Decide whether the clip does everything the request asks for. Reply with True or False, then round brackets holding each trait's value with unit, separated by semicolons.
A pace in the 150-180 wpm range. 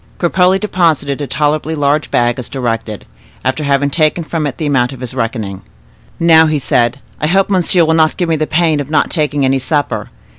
False (200 wpm)